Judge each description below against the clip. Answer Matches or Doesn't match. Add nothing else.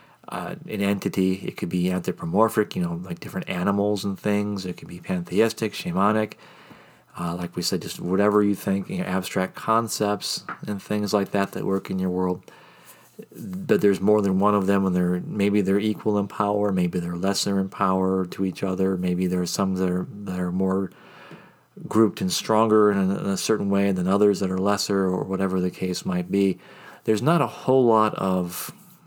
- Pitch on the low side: Matches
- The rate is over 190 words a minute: Matches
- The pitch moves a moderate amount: Doesn't match